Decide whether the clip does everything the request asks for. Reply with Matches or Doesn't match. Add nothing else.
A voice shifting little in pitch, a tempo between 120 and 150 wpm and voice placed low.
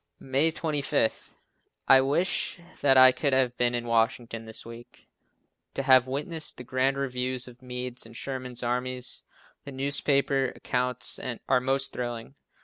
Matches